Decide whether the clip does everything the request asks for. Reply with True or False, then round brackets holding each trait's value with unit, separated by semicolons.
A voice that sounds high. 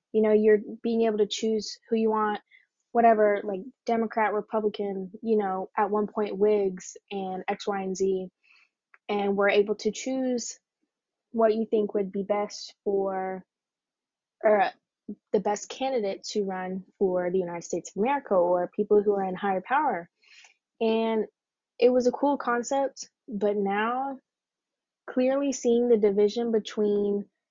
True (210 Hz)